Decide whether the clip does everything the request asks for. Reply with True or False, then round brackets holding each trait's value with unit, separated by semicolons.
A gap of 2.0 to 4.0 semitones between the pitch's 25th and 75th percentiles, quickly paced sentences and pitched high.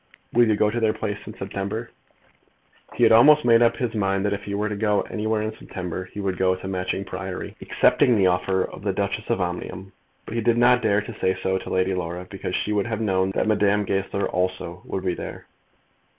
False (2.6 semitones; 220 wpm; 100 Hz)